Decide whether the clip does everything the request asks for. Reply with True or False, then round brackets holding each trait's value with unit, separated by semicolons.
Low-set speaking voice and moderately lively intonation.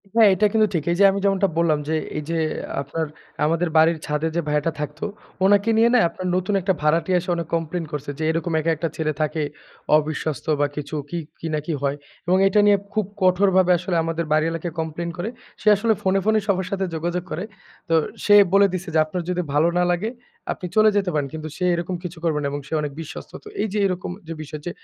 False (170 Hz; 3.3 semitones)